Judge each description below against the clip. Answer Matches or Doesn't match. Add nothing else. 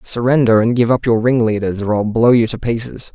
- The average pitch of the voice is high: Doesn't match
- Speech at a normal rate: Doesn't match